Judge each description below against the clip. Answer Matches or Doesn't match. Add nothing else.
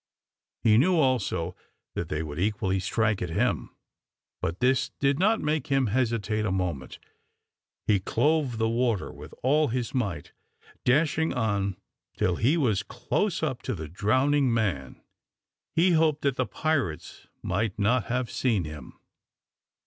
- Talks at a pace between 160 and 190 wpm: Doesn't match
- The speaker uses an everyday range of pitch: Doesn't match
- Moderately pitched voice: Doesn't match